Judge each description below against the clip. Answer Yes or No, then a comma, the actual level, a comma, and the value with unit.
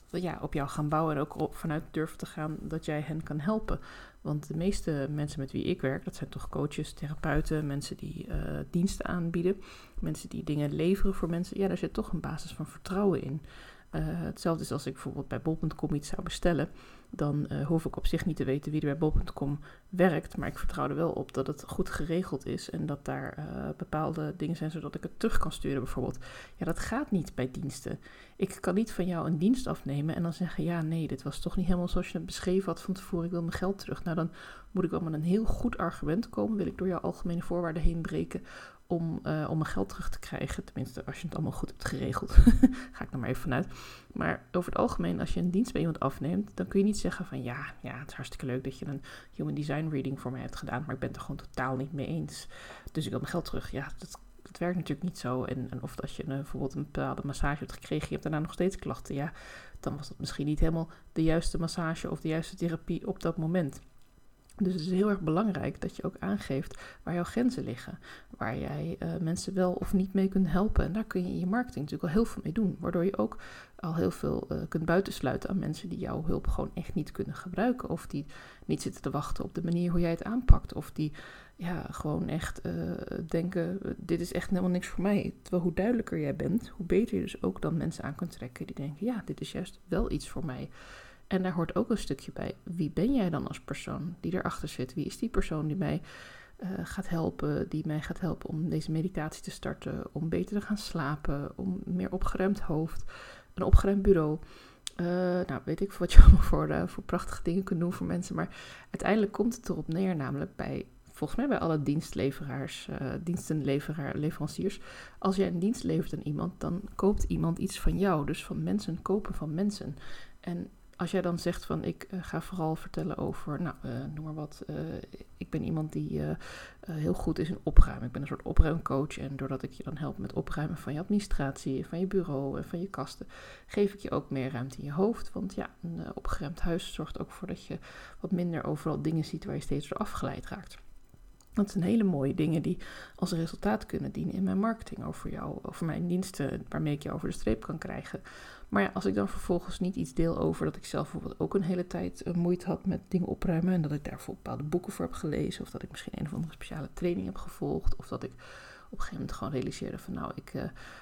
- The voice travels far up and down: No, average, 3.8 semitones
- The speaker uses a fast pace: Yes, fast, 235 wpm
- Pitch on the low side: No, medium, 170 Hz